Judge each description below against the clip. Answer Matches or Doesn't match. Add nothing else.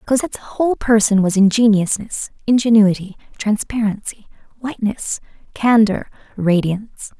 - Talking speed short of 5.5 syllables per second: Matches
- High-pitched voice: Matches